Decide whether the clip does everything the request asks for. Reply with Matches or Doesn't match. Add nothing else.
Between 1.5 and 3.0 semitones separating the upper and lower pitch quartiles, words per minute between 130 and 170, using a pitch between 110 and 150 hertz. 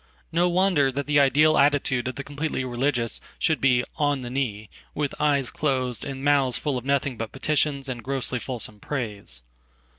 Matches